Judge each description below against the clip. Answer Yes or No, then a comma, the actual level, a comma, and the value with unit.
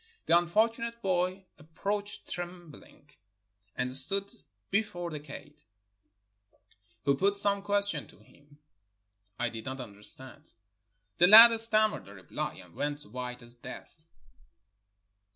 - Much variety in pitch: Yes, wide, 7.2 semitones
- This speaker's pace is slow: Yes, slow, 115 wpm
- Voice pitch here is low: No, medium, 170 Hz